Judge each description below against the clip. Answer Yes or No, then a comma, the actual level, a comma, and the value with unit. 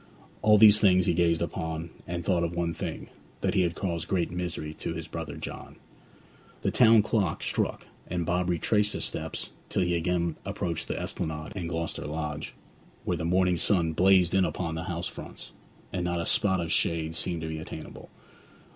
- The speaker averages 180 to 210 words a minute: Yes, average, 190 wpm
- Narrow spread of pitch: Yes, narrow, 2.0 semitones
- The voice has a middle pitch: No, very low, 85 Hz